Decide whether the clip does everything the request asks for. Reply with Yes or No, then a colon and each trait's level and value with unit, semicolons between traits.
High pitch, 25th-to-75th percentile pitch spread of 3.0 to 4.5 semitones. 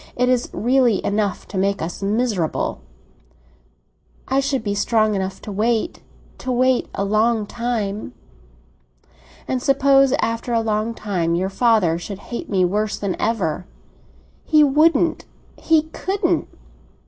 Yes: high, 220 Hz; average, 4.2 semitones